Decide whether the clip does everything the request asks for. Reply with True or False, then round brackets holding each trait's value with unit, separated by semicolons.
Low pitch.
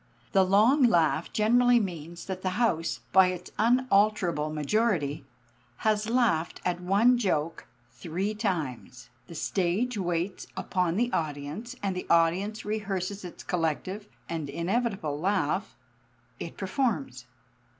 False (185 Hz)